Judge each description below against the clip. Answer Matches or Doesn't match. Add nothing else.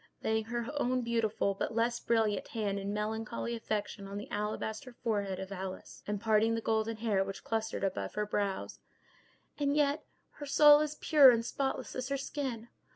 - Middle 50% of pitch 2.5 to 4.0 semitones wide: Matches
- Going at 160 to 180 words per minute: Matches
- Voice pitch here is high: Matches